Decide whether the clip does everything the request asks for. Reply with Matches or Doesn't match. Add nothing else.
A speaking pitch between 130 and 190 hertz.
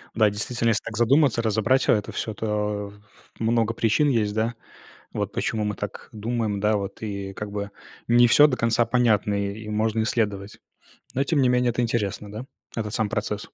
Doesn't match